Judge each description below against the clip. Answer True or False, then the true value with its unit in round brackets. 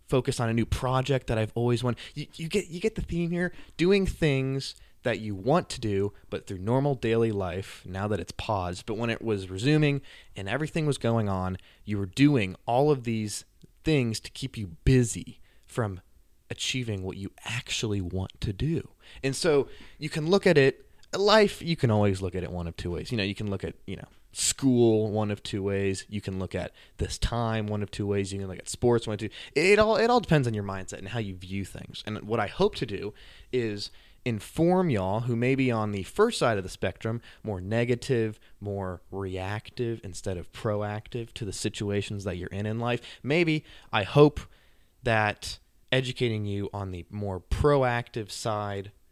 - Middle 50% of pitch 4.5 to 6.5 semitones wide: True (4.9 semitones)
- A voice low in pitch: True (110 Hz)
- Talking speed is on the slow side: False (205 wpm)